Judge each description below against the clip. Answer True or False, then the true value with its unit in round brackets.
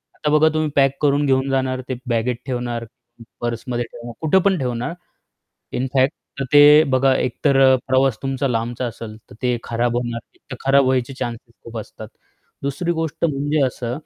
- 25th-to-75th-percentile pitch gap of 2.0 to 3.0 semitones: True (2.7 semitones)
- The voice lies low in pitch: True (130 Hz)